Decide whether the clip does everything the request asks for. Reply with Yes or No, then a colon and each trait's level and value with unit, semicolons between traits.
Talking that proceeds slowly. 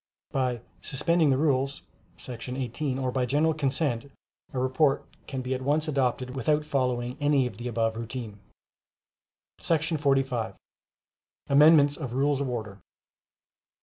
Yes: slow, 130 wpm